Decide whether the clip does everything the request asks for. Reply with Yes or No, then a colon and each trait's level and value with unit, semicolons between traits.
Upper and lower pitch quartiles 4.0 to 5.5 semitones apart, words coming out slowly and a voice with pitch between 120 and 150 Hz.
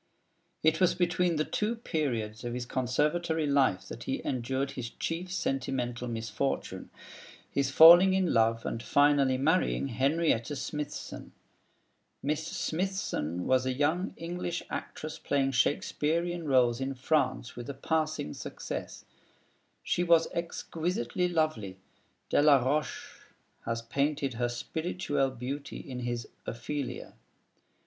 Yes: average, 4.6 semitones; slow, 120 wpm; medium, 140 Hz